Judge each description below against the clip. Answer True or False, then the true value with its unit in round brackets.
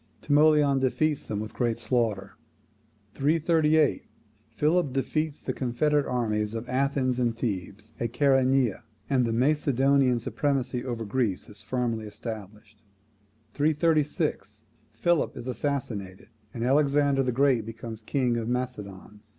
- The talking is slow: True (120 wpm)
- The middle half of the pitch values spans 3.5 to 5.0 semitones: True (4.0 semitones)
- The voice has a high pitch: False (125 Hz)